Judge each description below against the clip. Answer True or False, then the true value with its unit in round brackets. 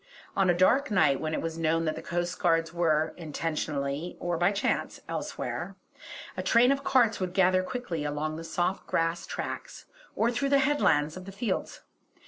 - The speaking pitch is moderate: True (175 Hz)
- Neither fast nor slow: True (175 wpm)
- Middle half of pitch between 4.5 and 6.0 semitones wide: False (4.0 semitones)